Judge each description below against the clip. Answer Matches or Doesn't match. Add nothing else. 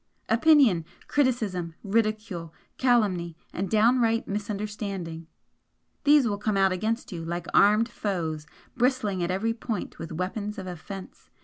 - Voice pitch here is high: Matches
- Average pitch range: Matches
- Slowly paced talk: Matches